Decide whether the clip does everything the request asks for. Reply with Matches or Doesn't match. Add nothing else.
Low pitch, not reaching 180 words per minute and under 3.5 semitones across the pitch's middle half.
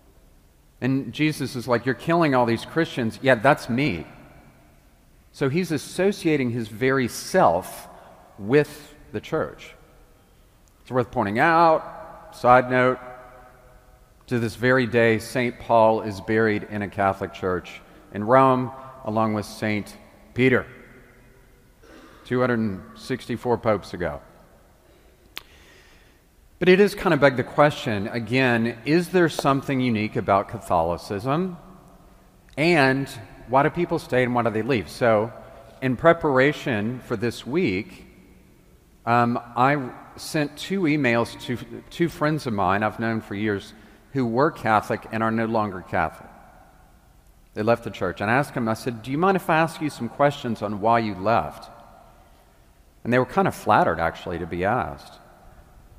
Doesn't match